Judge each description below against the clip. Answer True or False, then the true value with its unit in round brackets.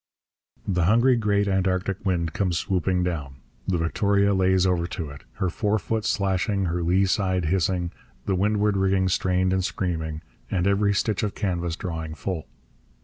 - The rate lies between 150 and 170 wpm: True (155 wpm)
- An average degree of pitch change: False (2.3 semitones)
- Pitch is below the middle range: True (95 Hz)